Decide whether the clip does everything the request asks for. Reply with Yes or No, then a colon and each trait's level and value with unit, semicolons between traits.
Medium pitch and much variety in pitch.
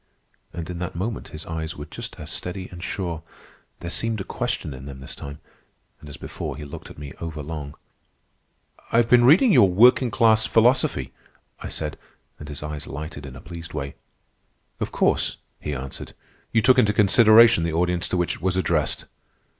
No: very low, 85 Hz; wide, 6.5 semitones